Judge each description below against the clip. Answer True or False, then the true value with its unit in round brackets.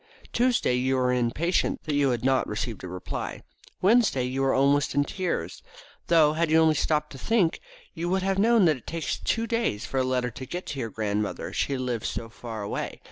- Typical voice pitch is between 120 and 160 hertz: True (140 Hz)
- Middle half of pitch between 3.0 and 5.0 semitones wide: False (5.4 semitones)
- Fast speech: True (210 wpm)